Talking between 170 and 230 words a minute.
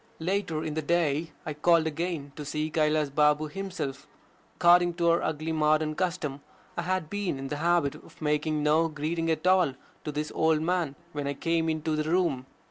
Yes: average, 190 wpm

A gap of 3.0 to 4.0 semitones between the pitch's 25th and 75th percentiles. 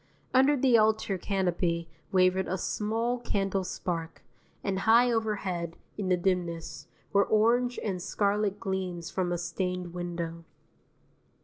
Yes: average, 3.5 semitones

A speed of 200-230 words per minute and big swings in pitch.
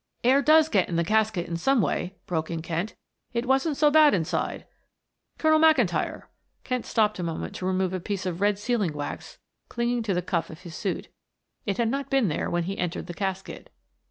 Yes: fast, 205 wpm; wide, 6.1 semitones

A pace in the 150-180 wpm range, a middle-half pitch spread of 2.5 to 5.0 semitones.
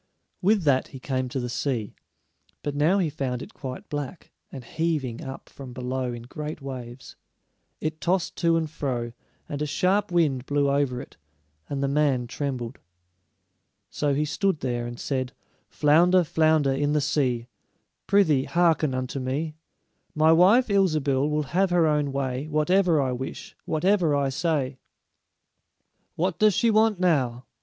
Yes: average, 155 wpm; average, 3.9 semitones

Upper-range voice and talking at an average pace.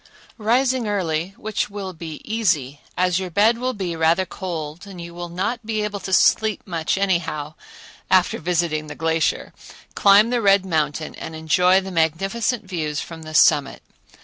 No: medium, 180 Hz; average, 155 wpm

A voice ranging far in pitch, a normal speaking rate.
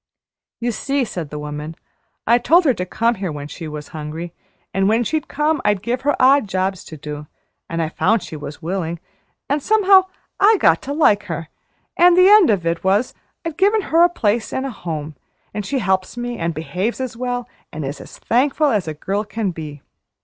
No: wide, 8.6 semitones; fast, 210 wpm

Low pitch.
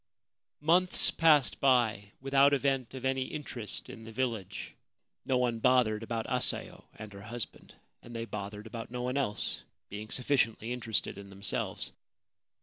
Yes: low, 120 Hz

